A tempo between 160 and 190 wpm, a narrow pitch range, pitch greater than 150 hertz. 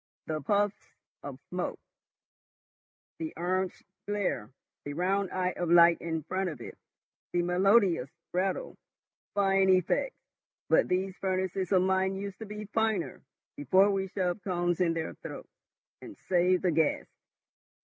No: average, 140 wpm; narrow, 2.0 semitones; medium, 185 Hz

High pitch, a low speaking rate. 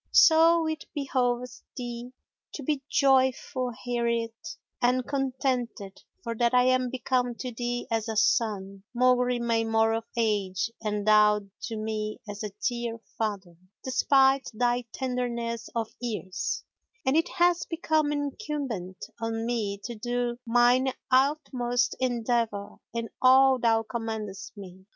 Yes: high, 240 Hz; slow, 130 wpm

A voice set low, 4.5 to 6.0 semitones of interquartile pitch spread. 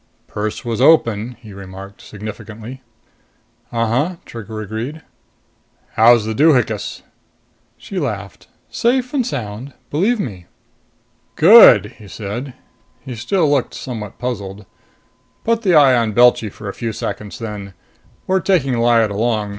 Yes: low, 115 Hz; average, 5.1 semitones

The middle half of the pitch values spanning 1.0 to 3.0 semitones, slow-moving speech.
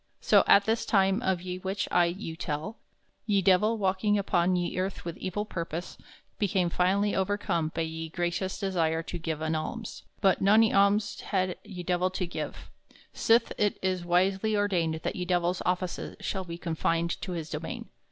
No: average, 2.7 semitones; average, 175 wpm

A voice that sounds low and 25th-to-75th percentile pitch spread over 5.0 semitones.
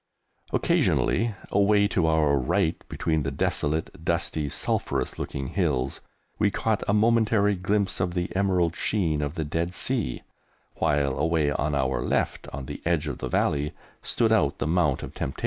Yes: very low, 80 Hz; wide, 5.5 semitones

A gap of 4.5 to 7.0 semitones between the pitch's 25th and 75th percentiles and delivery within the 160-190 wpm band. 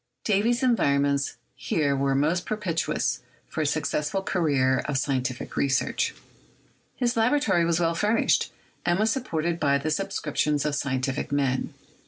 No: wide, 5.5 semitones; average, 140 wpm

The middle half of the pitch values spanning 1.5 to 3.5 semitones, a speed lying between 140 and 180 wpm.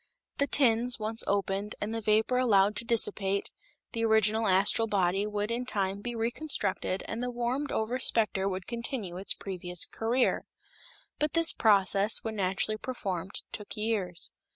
Yes: average, 3.1 semitones; average, 155 wpm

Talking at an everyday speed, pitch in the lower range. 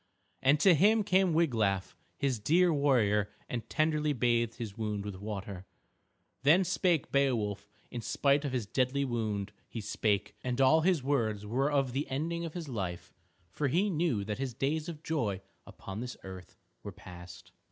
Yes: average, 170 wpm; low, 130 Hz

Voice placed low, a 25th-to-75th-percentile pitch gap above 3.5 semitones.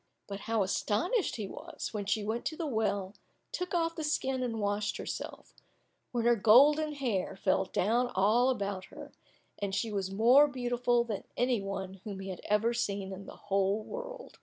No: high, 220 Hz; average, 4.1 semitones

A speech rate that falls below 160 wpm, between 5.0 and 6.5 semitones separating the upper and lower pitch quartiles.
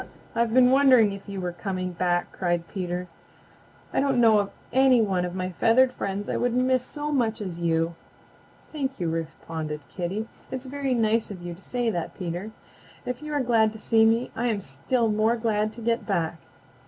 No: average, 195 wpm; wide, 5.5 semitones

